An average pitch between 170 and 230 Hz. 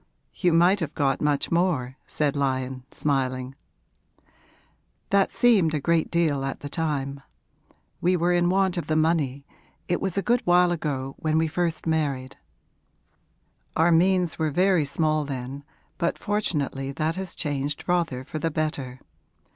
No: medium, 155 Hz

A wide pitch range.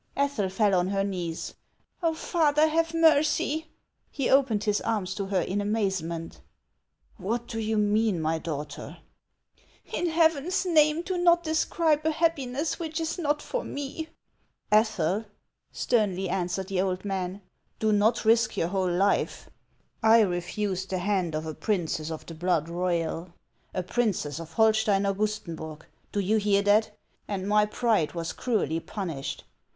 Yes: wide, 6.9 semitones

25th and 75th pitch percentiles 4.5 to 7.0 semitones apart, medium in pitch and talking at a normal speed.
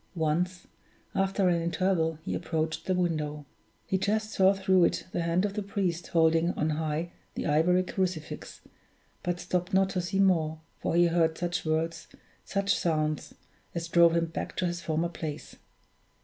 No: narrow, 2.5 semitones; medium, 170 Hz; average, 165 wpm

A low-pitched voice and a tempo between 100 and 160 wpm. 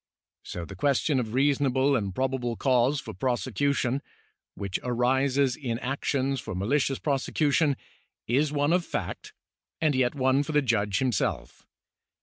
Yes: low, 130 Hz; average, 145 wpm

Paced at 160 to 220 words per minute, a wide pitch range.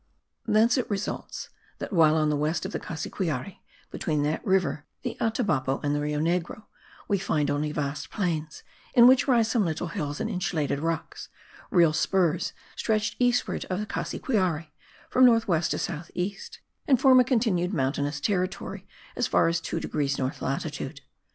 Yes: average, 170 wpm; wide, 5.8 semitones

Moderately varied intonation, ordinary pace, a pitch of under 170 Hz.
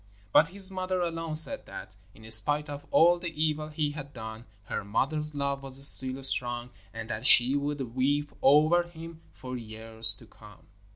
Yes: average, 4.6 semitones; average, 175 wpm; medium, 140 Hz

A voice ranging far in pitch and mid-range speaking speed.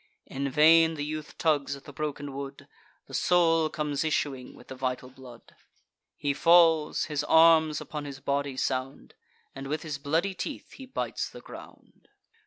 No: average, 2.7 semitones; average, 165 wpm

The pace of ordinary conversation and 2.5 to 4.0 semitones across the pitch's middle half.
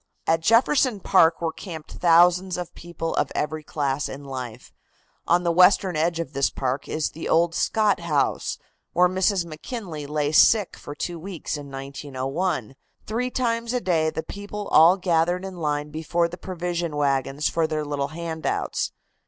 Yes: average, 165 wpm; average, 3.5 semitones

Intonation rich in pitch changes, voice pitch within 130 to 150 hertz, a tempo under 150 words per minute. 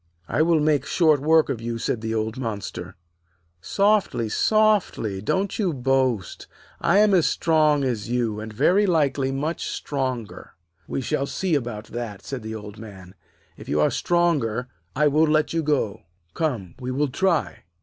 No: wide, 6.1 semitones; low, 135 Hz; average, 170 wpm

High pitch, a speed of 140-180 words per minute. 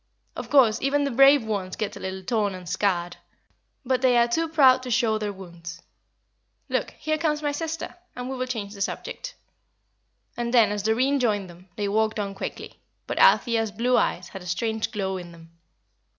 No: high, 220 Hz; average, 195 wpm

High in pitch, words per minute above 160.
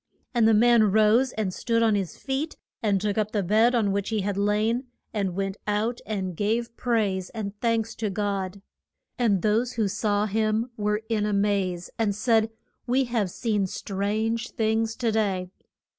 Yes: high, 215 Hz; average, 175 wpm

